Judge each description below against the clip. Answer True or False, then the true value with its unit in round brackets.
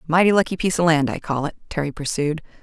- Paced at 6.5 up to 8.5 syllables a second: True (6.9 syllables/s)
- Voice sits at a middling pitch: True (160 Hz)